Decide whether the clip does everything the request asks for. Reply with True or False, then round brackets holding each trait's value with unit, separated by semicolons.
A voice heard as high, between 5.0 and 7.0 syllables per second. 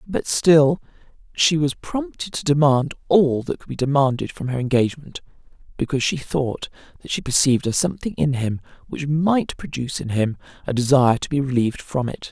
False (145 Hz; 5.5 syllables/s)